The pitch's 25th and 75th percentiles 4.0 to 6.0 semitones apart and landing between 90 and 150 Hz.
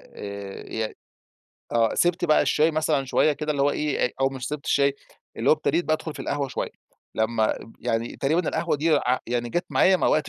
Yes: average, 4.3 semitones; medium, 140 Hz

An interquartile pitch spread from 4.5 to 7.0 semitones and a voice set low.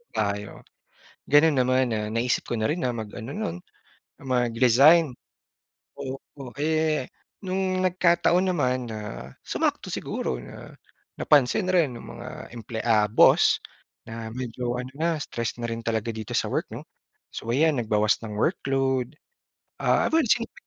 Yes: wide, 5.5 semitones; low, 125 Hz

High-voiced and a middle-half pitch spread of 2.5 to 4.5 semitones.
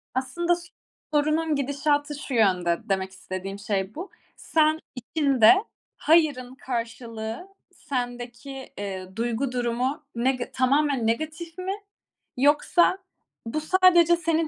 No: very high, 265 Hz; average, 5.1 semitones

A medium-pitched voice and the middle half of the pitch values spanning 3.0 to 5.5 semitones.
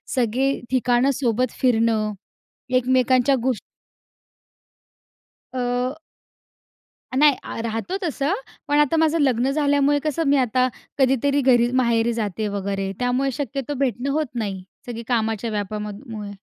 No: very high, 250 Hz; average, 3.5 semitones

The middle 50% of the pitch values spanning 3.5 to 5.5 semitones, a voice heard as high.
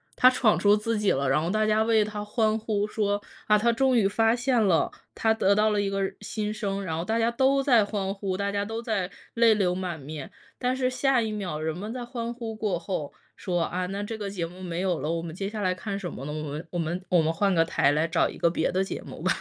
Yes: average, 3.9 semitones; high, 205 Hz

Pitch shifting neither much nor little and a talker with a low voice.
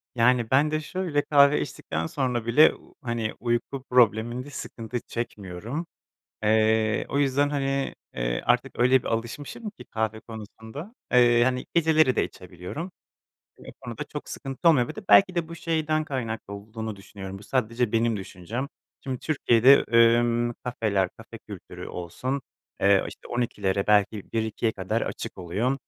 Yes: average, 4.1 semitones; low, 120 Hz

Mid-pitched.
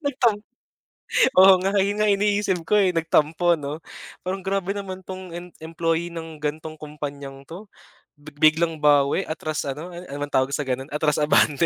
Yes: medium, 165 Hz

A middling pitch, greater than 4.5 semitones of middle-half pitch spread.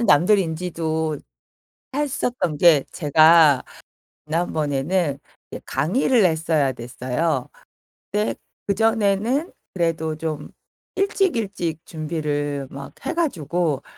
Yes: medium, 160 Hz; average, 5.1 semitones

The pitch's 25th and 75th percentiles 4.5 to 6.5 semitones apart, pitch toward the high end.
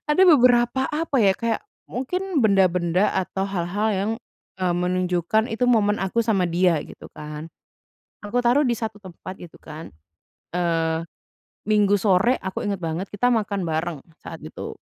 Yes: average, 4.8 semitones; high, 195 Hz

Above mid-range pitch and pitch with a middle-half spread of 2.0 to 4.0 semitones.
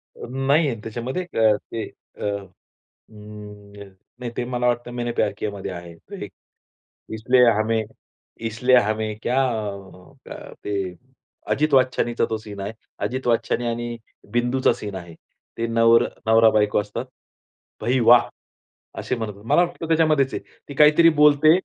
No: low, 120 Hz; average, 3.1 semitones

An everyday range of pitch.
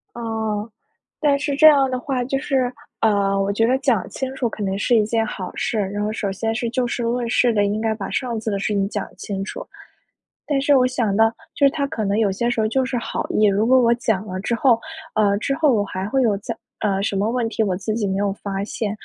Yes: average, 3.7 semitones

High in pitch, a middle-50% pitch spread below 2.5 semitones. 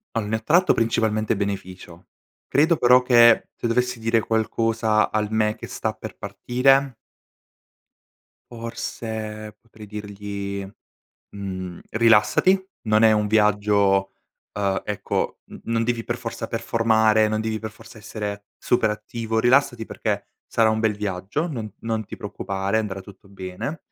No: low, 110 Hz; narrow, 2.0 semitones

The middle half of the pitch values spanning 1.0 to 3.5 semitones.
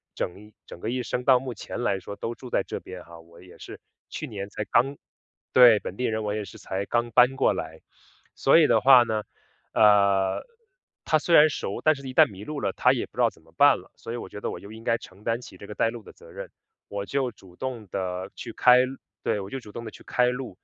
No: average, 4.1 semitones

